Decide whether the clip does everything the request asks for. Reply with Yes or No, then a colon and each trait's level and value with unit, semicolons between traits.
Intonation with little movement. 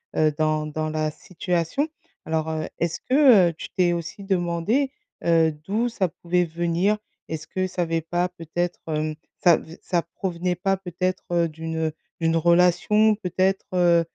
Yes: narrow, 2.3 semitones